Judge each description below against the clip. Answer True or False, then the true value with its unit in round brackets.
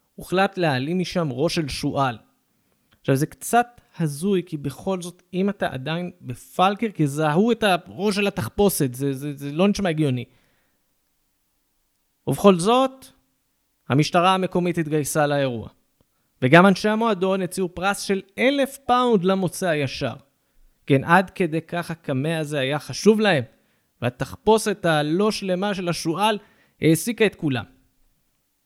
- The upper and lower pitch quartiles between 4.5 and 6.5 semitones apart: True (5.6 semitones)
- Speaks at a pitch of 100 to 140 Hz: False (175 Hz)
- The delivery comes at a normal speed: True (130 wpm)